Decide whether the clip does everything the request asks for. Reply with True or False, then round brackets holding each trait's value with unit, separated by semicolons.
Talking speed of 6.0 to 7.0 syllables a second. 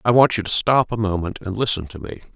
True (6.2 syllables/s)